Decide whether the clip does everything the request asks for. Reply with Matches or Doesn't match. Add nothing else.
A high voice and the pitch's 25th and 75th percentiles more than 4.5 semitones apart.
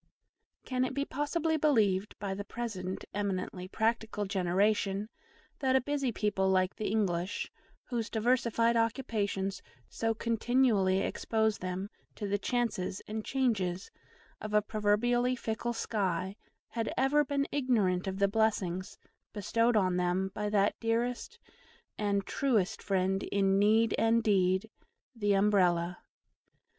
Doesn't match